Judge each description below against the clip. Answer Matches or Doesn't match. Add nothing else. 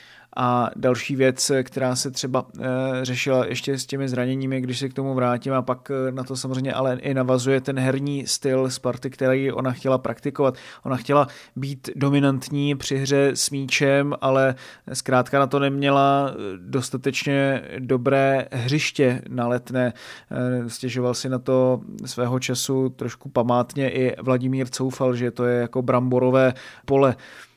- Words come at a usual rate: Matches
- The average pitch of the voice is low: Matches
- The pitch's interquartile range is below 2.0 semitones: Matches